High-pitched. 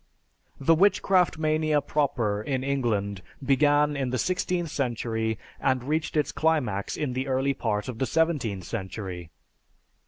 No: low, 135 Hz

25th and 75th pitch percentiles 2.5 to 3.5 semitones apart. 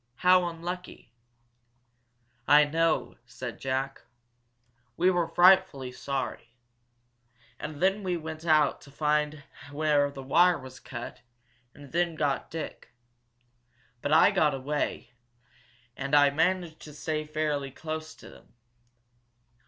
Yes: average, 2.9 semitones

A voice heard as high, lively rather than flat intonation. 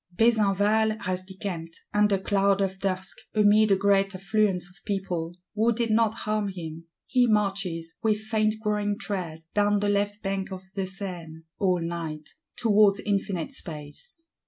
No: high, 200 Hz; narrow, 2.5 semitones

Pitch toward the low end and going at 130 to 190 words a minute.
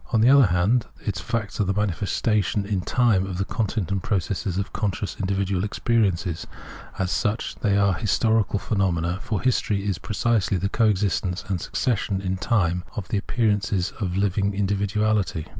Yes: low, 100 Hz; average, 170 wpm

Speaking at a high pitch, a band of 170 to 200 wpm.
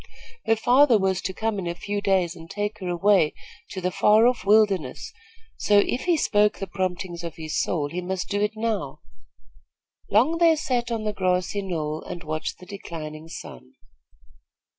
Yes: high, 195 Hz; average, 180 wpm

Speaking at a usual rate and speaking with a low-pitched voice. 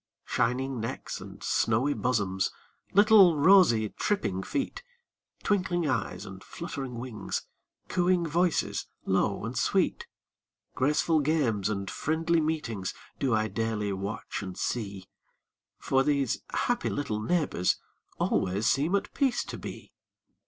No: slow, 120 wpm; low, 130 Hz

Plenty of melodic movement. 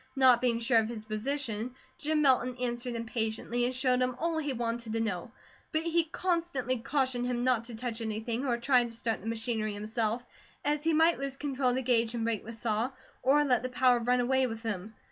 No: narrow, 2.6 semitones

